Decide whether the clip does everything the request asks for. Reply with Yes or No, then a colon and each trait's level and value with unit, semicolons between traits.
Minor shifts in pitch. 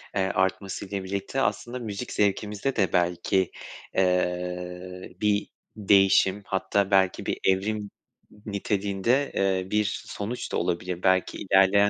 Yes: narrow, 1.7 semitones